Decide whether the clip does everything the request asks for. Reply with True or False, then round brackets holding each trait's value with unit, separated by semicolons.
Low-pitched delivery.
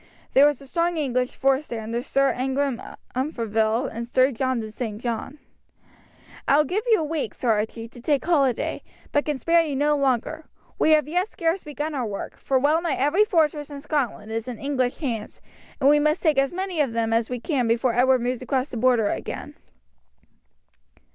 False (270 Hz)